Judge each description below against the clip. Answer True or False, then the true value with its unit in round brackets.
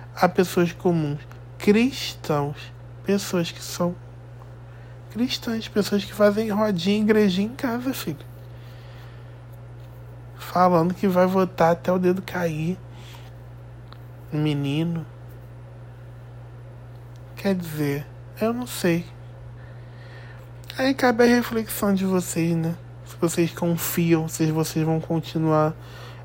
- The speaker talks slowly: True (100 wpm)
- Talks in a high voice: False (150 Hz)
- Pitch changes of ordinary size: False (6.9 semitones)